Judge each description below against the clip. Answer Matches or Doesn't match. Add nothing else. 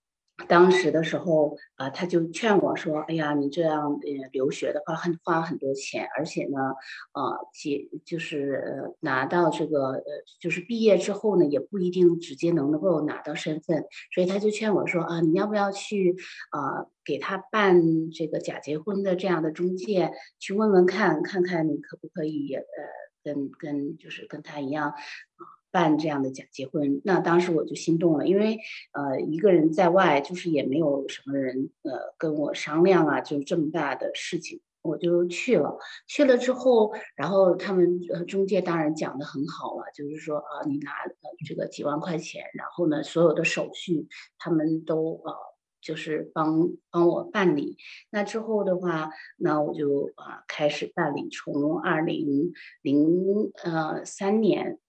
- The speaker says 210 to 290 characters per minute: Matches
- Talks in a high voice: Doesn't match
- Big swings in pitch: Doesn't match